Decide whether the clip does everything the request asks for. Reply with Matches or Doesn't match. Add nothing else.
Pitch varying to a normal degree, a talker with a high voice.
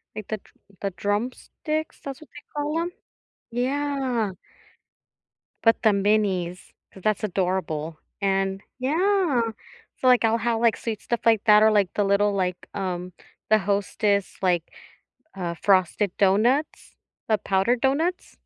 Matches